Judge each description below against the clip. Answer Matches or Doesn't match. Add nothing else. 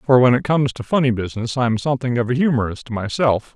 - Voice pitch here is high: Doesn't match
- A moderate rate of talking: Doesn't match